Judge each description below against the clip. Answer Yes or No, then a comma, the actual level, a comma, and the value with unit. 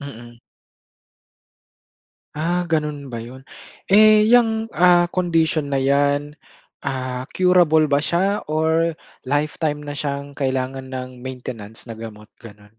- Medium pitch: Yes, medium, 145 Hz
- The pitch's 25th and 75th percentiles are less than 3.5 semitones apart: No, average, 4.5 semitones